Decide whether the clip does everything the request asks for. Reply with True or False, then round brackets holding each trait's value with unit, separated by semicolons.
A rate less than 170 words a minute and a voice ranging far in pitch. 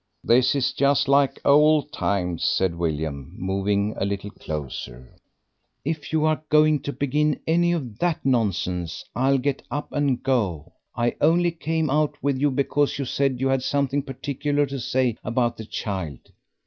True (160 wpm; 6.3 semitones)